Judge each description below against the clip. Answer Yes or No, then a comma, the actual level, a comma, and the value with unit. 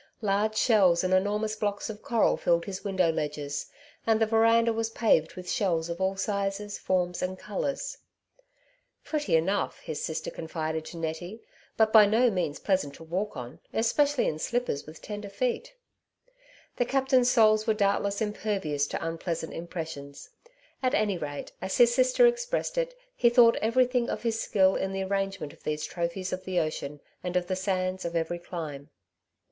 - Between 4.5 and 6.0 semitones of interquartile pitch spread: Yes, average, 4.8 semitones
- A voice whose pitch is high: Yes, high, 195 Hz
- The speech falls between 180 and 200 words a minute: Yes, average, 185 wpm